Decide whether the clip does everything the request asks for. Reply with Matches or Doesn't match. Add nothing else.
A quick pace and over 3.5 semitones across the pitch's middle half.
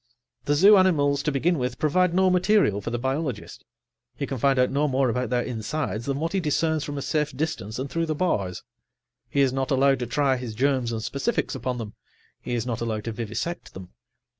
Matches